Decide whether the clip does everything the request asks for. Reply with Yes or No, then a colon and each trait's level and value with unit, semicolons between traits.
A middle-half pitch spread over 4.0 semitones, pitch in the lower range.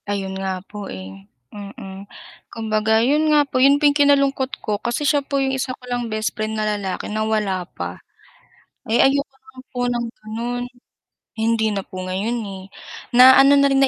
No: average, 4.7 semitones; high, 230 Hz